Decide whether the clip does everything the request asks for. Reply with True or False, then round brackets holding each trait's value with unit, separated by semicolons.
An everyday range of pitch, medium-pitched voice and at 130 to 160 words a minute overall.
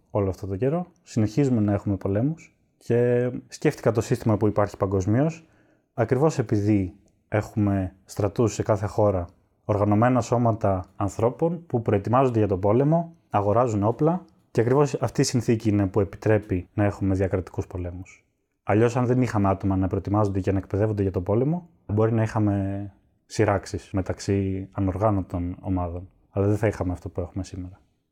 False (3.9 semitones; 105 Hz; 155 wpm)